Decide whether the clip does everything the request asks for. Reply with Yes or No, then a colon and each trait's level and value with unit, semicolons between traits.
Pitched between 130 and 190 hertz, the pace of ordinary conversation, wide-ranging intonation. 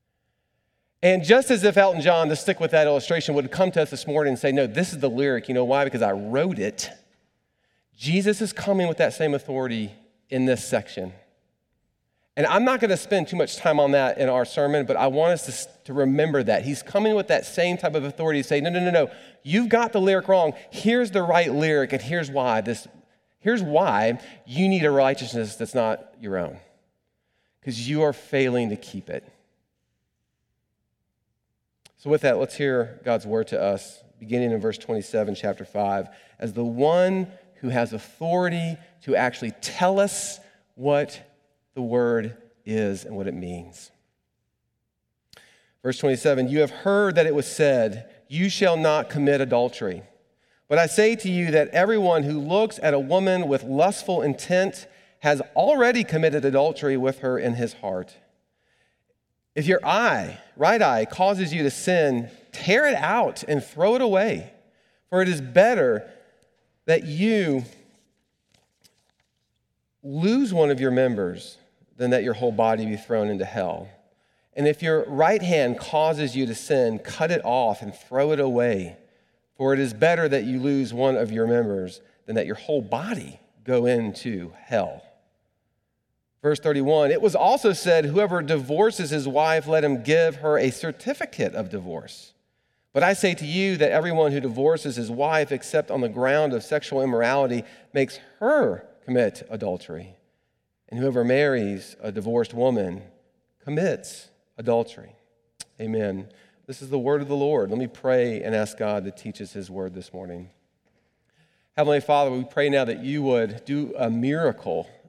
Yes: medium, 140 Hz; average, 170 wpm; wide, 5.7 semitones